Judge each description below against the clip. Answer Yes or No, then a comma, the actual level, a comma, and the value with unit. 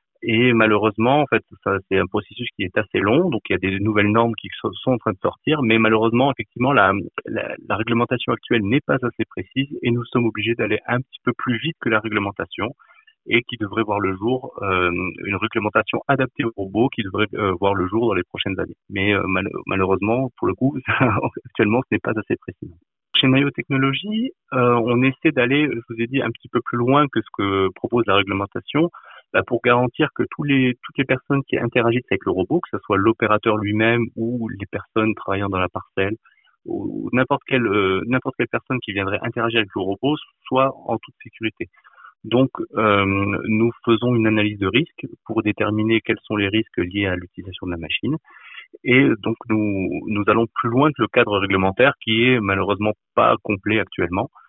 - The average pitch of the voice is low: Yes, low, 115 Hz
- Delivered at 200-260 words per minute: Yes, average, 205 wpm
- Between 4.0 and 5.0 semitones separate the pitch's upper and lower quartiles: No, average, 3.5 semitones